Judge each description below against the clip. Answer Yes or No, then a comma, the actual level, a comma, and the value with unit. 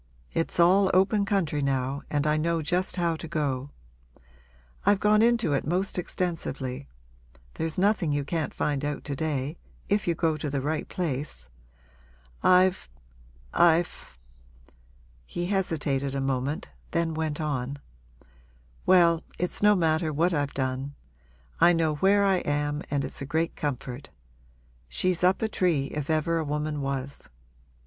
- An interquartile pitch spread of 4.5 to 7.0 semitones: No, average, 3.9 semitones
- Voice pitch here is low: No, medium, 155 Hz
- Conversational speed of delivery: Yes, average, 150 wpm